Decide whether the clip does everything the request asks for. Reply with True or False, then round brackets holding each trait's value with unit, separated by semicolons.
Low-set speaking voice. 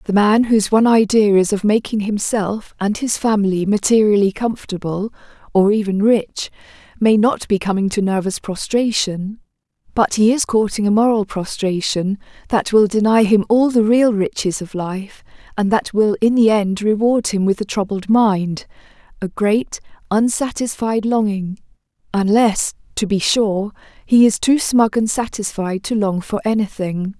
False (210 Hz)